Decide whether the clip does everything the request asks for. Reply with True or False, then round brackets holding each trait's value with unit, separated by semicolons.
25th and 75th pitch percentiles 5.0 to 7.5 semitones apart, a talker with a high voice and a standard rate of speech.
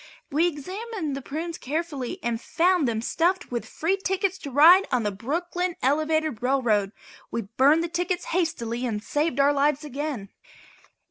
True (5.6 semitones; 295 Hz; 155 wpm)